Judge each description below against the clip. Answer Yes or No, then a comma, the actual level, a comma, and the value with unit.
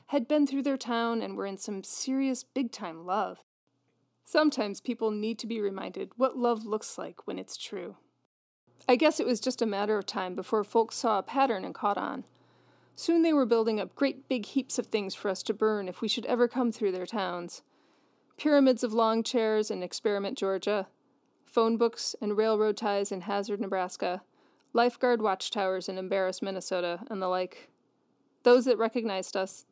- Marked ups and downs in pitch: No, average, 3.9 semitones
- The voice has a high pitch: Yes, high, 220 Hz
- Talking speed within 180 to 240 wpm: Yes, average, 185 wpm